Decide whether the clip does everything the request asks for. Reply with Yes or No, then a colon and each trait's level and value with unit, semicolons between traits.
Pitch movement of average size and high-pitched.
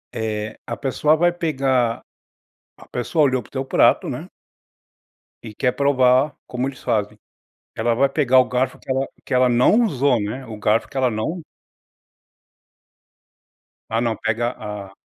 No: average, 3.2 semitones; low, 125 Hz